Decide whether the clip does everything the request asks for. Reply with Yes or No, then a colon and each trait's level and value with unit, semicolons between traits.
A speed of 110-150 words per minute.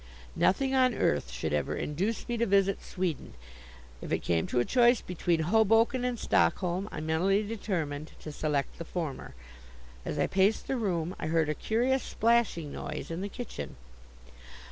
No: average, 165 wpm